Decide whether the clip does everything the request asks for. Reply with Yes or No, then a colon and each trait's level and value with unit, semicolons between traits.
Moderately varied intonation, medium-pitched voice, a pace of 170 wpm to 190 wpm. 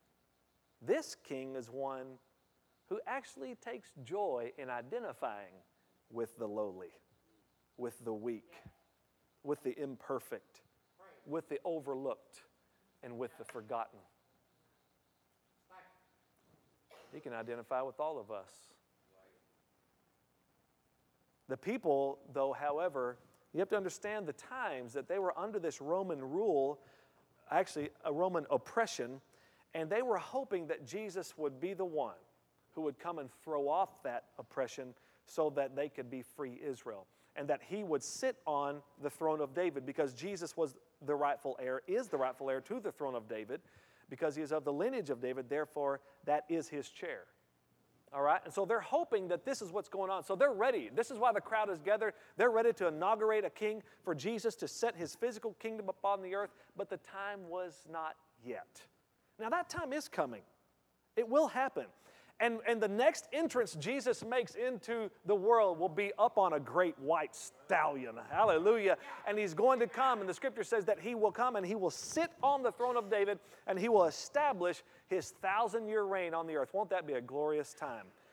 No: wide, 7.8 semitones; medium, 170 Hz; average, 175 wpm